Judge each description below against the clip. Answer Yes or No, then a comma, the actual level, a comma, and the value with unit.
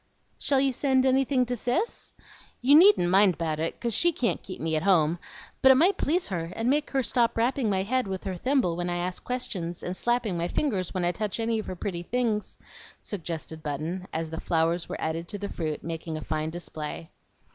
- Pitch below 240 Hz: Yes, high, 190 Hz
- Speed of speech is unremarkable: No, fast, 215 wpm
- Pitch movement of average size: No, wide, 6.9 semitones